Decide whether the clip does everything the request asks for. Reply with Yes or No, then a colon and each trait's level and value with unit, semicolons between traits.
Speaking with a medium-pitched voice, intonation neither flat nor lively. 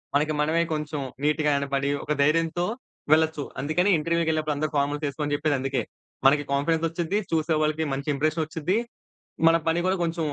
No: medium, 155 Hz; narrow, 2.1 semitones